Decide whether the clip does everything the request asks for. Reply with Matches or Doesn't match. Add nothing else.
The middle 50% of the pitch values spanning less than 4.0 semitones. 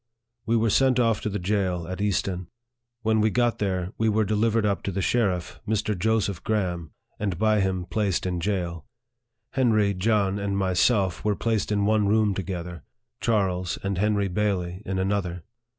Matches